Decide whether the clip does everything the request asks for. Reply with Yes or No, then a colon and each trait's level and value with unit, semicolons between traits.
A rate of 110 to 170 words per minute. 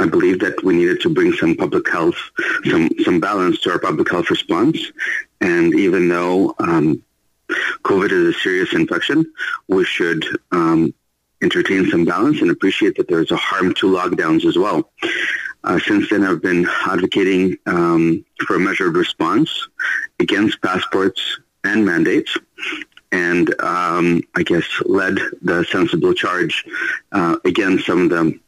Yes: average, 150 wpm